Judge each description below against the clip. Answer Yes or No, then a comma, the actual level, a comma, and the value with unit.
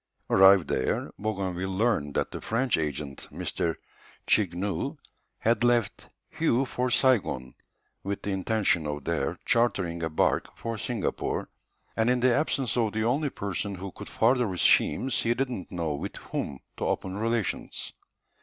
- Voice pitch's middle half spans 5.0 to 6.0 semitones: Yes, wide, 5.5 semitones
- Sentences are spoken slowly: No, average, 155 wpm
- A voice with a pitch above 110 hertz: No, low, 100 Hz